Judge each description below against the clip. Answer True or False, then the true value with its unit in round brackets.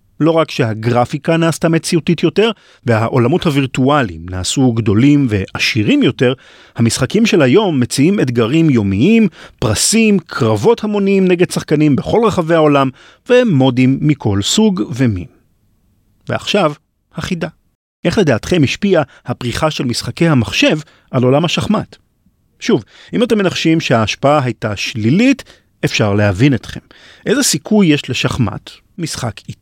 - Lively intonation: True (6.5 semitones)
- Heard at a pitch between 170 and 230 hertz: False (145 Hz)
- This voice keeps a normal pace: True (115 wpm)